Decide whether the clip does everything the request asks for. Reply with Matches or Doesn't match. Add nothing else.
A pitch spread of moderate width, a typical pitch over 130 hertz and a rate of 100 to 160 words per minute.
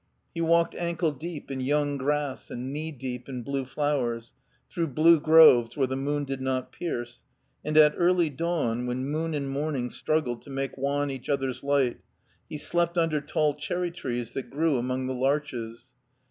Doesn't match